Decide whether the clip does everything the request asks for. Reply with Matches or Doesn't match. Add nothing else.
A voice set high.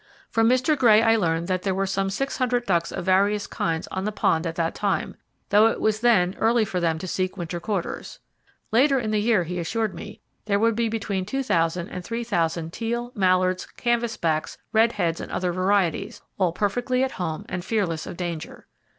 Matches